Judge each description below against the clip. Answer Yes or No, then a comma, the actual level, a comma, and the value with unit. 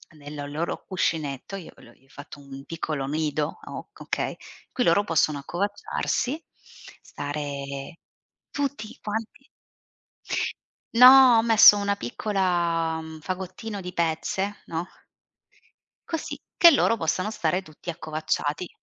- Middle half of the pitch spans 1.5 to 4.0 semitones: No, average, 5.3 semitones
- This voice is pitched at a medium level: Yes, medium, 170 Hz